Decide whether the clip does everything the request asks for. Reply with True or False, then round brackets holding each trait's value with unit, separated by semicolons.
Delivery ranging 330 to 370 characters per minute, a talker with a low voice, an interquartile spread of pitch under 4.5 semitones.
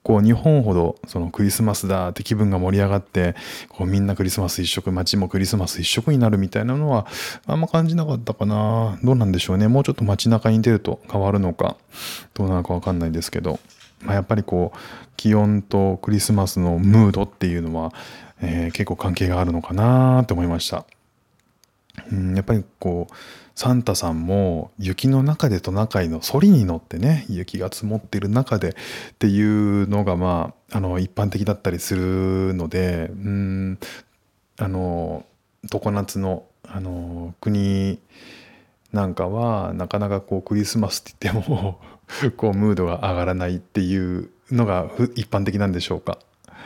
True (340 characters per minute; 100 Hz; 2.9 semitones)